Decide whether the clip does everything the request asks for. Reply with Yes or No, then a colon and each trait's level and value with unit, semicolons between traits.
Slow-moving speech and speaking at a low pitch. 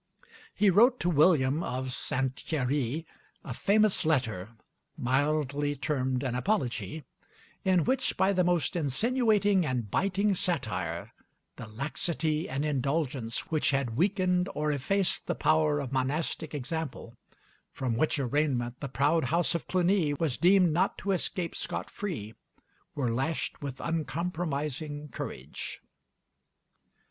No: slow, 125 wpm; medium, 150 Hz